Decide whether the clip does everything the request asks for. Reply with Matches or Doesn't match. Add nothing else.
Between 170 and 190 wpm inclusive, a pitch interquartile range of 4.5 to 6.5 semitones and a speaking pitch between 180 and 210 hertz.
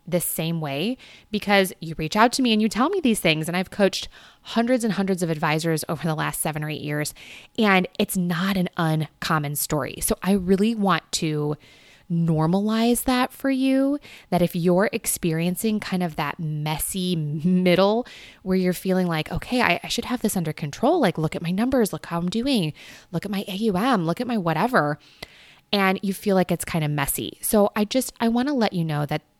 Doesn't match